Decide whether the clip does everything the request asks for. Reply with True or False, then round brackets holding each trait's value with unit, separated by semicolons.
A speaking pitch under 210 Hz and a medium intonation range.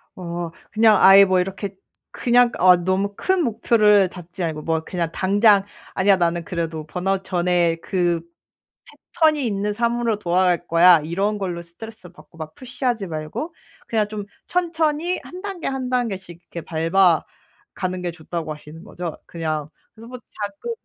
True (190 Hz; 4.7 semitones)